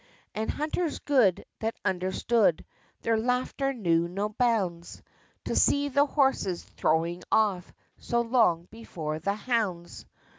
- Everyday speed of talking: No, slow, 120 wpm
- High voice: Yes, high, 215 Hz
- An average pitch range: No, wide, 5.9 semitones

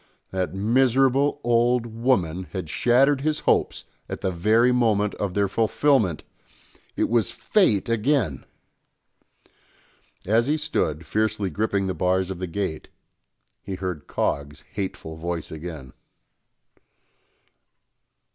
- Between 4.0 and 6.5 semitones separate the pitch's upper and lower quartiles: Yes, average, 5.0 semitones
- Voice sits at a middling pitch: No, low, 105 Hz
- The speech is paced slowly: Yes, slow, 115 wpm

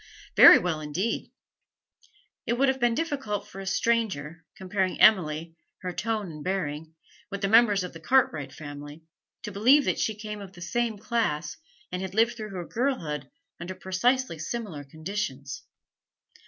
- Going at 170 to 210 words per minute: No, average, 155 wpm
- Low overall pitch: No, high, 195 Hz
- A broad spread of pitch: Yes, wide, 6.0 semitones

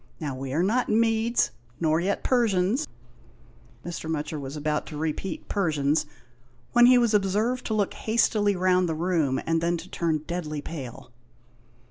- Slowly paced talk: No, average, 170 wpm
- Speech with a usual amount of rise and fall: No, wide, 5.7 semitones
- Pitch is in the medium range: Yes, medium, 175 Hz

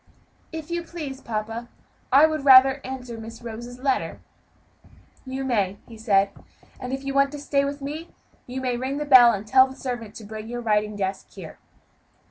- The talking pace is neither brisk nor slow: Yes, average, 185 wpm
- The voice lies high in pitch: Yes, very high, 255 Hz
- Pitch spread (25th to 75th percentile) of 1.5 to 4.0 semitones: Yes, average, 3.6 semitones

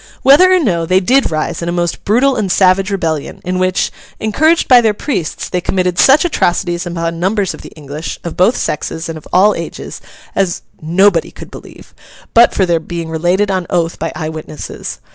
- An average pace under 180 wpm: No, average, 195 wpm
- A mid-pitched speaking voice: Yes, medium, 180 Hz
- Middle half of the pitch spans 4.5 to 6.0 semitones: No, average, 3.7 semitones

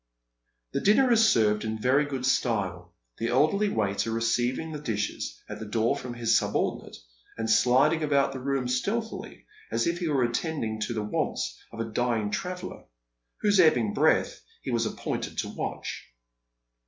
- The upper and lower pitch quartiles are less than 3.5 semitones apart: No, wide, 5.5 semitones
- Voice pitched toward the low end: Yes, low, 125 Hz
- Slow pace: No, average, 165 wpm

